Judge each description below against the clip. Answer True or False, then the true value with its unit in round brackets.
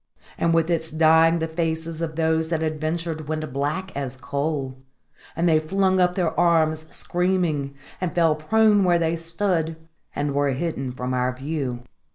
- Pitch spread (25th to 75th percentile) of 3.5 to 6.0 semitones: False (2.4 semitones)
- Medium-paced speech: True (170 wpm)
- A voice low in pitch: False (160 Hz)